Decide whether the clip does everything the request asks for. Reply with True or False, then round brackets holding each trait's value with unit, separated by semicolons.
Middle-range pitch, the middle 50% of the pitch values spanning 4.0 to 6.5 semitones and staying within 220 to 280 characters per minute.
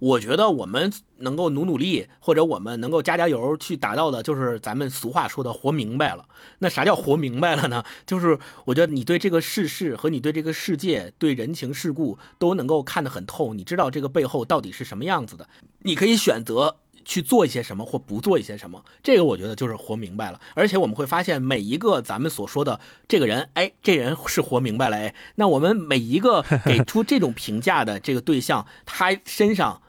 False (155 Hz; 5.2 semitones; 330 characters per minute)